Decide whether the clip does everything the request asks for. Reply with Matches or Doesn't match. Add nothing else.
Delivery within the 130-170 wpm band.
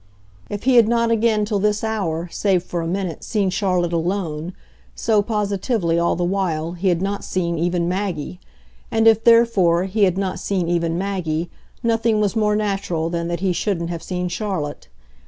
Doesn't match